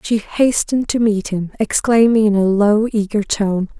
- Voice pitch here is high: Yes, high, 210 Hz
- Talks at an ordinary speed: Yes, average, 175 wpm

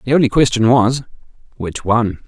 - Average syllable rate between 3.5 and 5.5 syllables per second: No, 5.7 syllables/s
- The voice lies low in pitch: Yes, low, 120 Hz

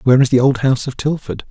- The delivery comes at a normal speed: No, fast, 280 wpm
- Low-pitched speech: Yes, low, 130 Hz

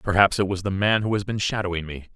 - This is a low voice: Yes, very low, 95 Hz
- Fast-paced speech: Yes, fast, 280 wpm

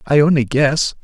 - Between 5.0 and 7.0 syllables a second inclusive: No, 4.7 syllables/s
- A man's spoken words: Yes, male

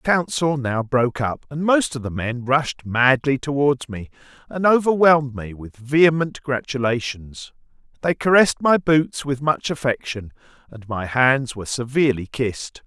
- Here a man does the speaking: Yes, male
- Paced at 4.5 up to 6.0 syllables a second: Yes, 4.8 syllables/s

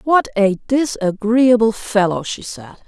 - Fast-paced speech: No, slow, 125 wpm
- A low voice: No, high, 220 Hz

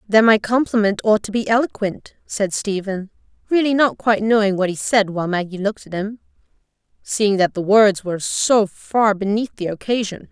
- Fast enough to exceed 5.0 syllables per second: Yes, 5.3 syllables/s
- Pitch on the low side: No, high, 205 Hz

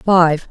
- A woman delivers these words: Yes, female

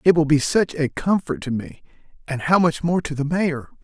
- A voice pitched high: No, medium, 150 Hz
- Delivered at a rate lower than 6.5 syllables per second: Yes, 5.0 syllables/s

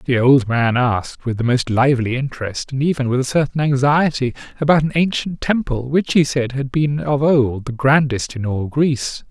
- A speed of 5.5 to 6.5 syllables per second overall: No, 5.0 syllables/s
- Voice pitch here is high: No, low, 135 Hz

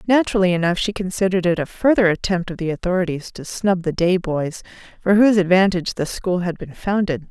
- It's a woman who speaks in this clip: Yes, female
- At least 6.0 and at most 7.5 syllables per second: Yes, 6.1 syllables/s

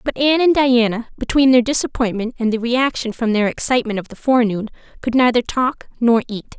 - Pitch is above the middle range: Yes, high, 240 Hz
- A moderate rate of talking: Yes, average, 190 wpm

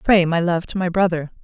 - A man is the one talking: No, female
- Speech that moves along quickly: Yes, fast, 250 wpm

